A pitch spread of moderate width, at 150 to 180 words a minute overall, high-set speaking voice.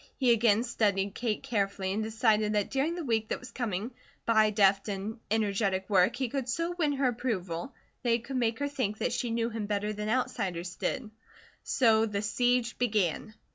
No: average, 3.2 semitones; average, 190 wpm; high, 220 Hz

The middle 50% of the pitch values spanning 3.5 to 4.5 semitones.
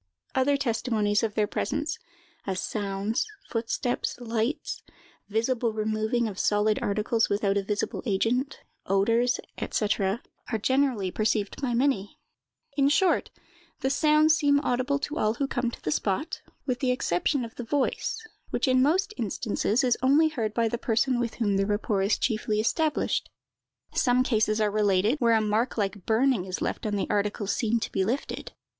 Yes: average, 4.0 semitones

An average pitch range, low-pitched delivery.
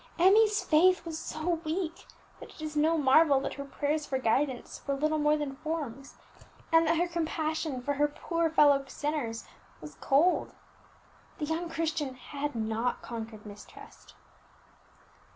No: average, 3.1 semitones; very high, 300 Hz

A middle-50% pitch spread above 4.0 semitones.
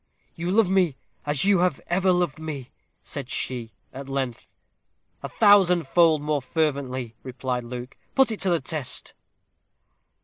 Yes: wide, 5.4 semitones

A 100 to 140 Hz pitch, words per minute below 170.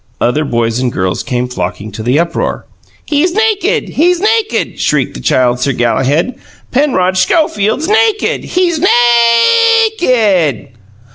No: high, 220 Hz; average, 140 wpm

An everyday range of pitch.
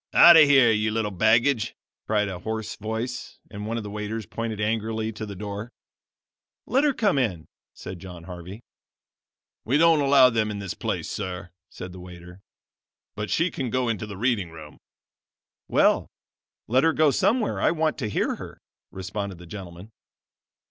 Yes: average, 4.5 semitones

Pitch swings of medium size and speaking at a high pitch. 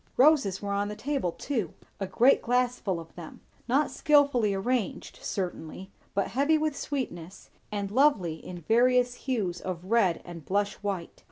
No: wide, 5.7 semitones; high, 205 Hz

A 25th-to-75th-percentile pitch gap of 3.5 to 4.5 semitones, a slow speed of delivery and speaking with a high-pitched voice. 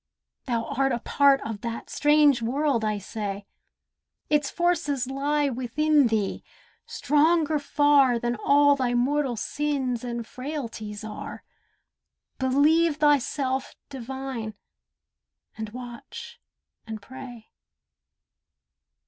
Yes: average, 3.8 semitones; slow, 100 wpm; very high, 265 Hz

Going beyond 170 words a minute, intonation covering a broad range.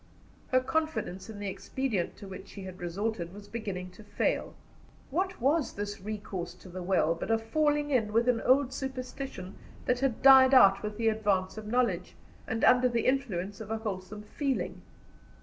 No: average, 180 wpm; average, 4.9 semitones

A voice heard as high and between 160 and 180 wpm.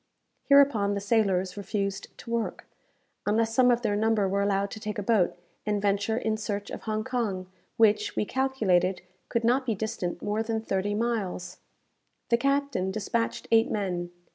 Yes: high, 210 Hz; average, 165 wpm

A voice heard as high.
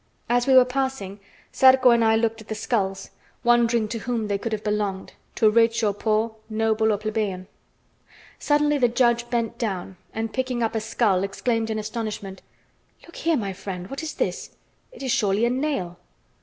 Yes: high, 225 Hz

